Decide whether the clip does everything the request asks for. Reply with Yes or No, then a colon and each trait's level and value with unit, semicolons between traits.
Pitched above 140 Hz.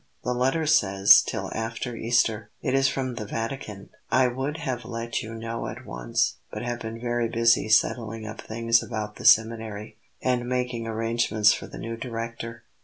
No: low, 115 Hz